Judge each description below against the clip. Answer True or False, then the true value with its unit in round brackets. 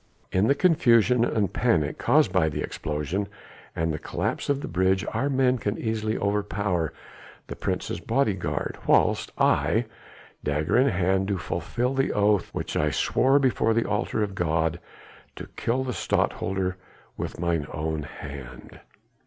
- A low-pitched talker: True (100 Hz)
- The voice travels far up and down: True (6.3 semitones)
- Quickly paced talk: False (150 wpm)